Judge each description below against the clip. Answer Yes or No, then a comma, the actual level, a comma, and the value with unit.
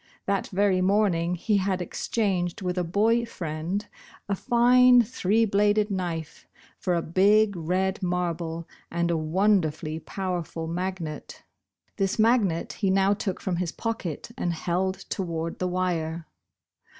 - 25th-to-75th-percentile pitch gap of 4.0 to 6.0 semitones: No, average, 3.1 semitones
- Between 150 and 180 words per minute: No, slow, 135 wpm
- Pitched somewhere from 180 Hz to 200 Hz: Yes, medium, 185 Hz